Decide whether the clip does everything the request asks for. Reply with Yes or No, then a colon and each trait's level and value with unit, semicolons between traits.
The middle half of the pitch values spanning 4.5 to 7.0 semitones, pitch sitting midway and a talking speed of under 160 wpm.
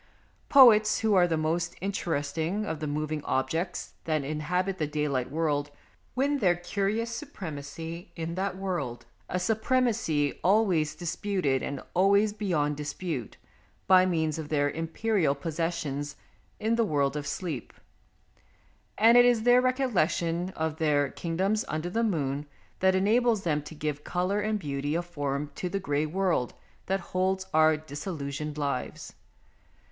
Yes: average, 4.9 semitones; medium, 170 Hz; average, 140 wpm